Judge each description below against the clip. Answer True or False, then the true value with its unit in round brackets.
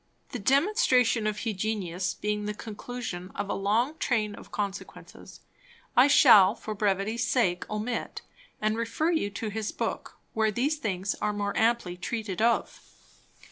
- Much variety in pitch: False (2.8 semitones)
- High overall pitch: True (215 Hz)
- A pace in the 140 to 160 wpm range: True (145 wpm)